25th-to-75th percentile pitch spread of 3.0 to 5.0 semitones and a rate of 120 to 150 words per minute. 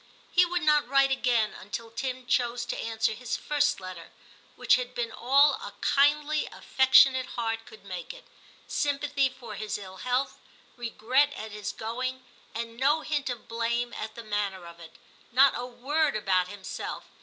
No: average, 3.9 semitones; average, 165 wpm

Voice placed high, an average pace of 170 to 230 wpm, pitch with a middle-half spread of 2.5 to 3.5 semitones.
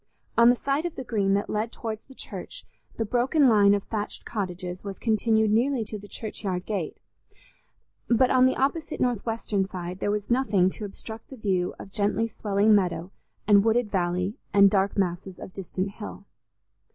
Yes: high, 210 Hz; average, 175 wpm; average, 3.1 semitones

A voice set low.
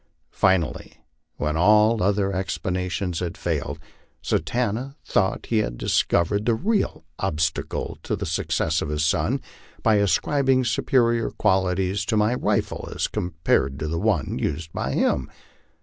Yes: very low, 95 Hz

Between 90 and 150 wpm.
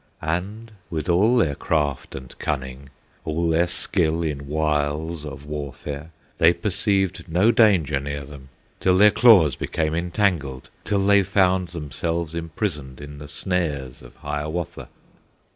Yes: slow, 135 wpm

